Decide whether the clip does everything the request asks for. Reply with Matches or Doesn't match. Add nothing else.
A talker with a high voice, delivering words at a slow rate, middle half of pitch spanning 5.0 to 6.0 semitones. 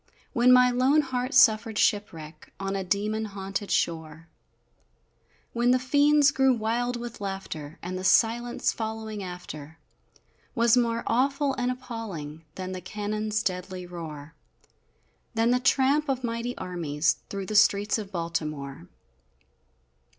Matches